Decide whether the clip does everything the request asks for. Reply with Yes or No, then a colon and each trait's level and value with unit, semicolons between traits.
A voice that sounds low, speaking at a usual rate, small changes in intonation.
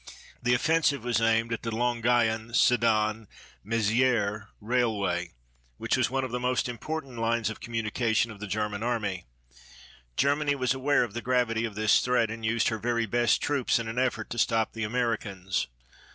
Yes: low, 115 Hz; average, 170 wpm; narrow, 2.2 semitones